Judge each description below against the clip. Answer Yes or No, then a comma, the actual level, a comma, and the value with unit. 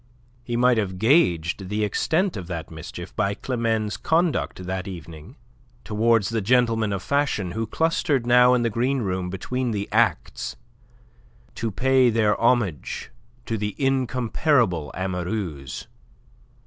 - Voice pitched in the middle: No, low, 110 Hz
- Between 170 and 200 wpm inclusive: No, slow, 135 wpm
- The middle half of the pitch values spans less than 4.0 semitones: No, average, 4.9 semitones